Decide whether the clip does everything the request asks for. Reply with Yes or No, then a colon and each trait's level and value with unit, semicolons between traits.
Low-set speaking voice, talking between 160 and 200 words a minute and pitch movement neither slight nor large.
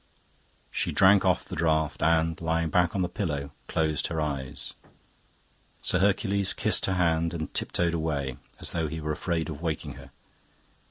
No: very low, 80 Hz; average, 165 wpm; narrow, 2.1 semitones